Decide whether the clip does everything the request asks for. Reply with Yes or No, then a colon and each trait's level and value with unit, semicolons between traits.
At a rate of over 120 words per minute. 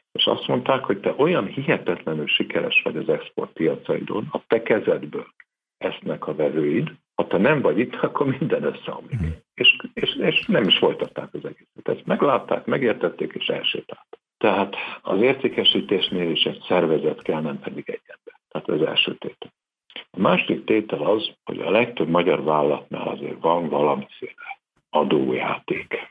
Yes: average, 150 wpm